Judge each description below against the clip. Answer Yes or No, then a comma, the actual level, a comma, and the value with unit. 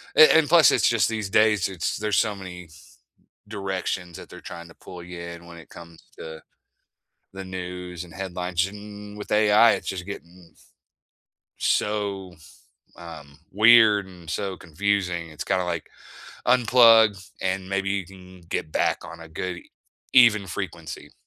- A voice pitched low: Yes, very low, 95 Hz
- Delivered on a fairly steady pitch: No, average, 3.2 semitones